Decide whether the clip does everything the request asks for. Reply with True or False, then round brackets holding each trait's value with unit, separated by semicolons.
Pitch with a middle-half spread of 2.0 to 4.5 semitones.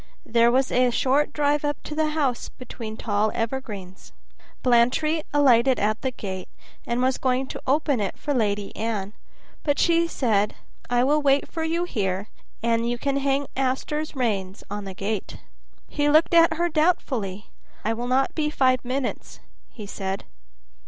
False (5.1 semitones)